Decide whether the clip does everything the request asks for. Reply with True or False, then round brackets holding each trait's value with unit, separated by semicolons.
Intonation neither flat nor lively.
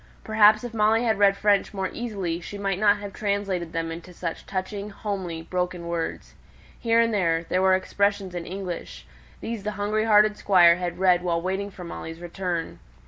True (3.0 semitones)